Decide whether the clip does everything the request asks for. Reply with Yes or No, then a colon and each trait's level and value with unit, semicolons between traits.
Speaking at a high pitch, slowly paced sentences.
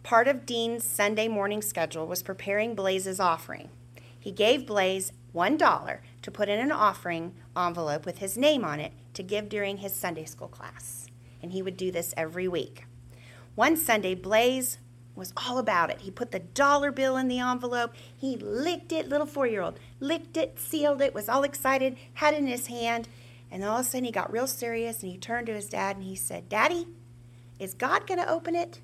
No: high, 205 Hz; fast, 205 wpm